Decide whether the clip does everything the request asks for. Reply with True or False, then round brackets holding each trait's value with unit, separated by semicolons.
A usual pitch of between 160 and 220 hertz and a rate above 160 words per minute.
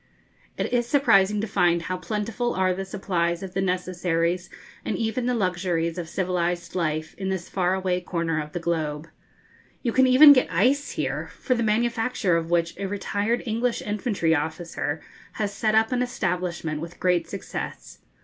True (185 Hz; 170 wpm)